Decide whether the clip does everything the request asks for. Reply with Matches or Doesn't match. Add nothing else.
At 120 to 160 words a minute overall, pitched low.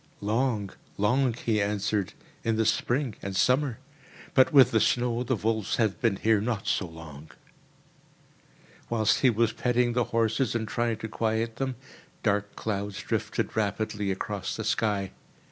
Matches